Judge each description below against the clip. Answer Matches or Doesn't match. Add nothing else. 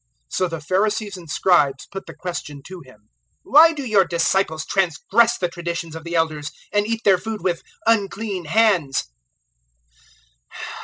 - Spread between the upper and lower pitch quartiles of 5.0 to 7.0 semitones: Doesn't match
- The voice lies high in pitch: Doesn't match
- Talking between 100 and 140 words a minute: Doesn't match